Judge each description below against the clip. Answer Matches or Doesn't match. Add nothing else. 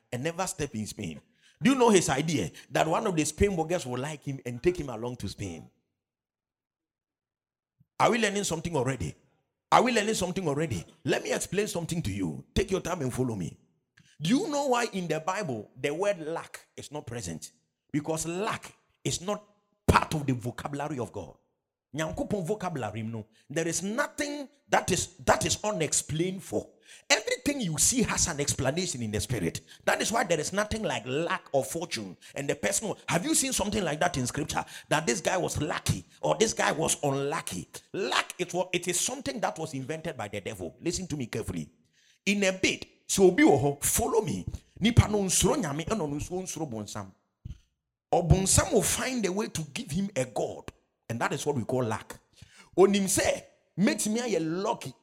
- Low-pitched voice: Doesn't match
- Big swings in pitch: Matches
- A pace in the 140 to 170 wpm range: Doesn't match